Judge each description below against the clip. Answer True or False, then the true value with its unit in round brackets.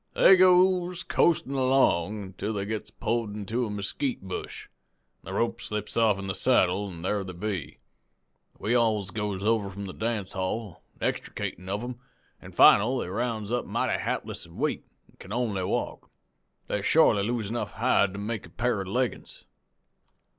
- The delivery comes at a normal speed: True (170 wpm)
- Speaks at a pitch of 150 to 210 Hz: False (105 Hz)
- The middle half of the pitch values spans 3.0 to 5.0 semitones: True (3.5 semitones)